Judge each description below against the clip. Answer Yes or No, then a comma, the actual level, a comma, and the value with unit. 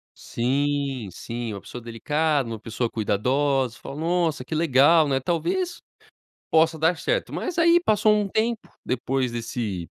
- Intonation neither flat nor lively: No, wide, 5.9 semitones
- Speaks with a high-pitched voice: No, medium, 140 Hz